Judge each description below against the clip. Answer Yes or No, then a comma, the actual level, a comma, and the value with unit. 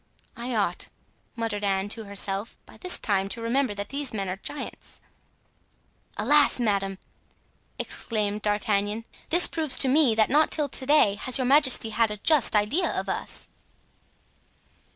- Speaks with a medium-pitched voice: No, high, 225 Hz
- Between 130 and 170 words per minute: Yes, average, 150 wpm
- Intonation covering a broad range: No, average, 4.8 semitones